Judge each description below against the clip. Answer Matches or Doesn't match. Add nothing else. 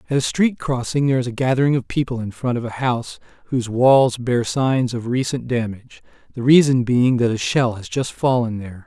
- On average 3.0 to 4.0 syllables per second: Doesn't match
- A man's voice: Matches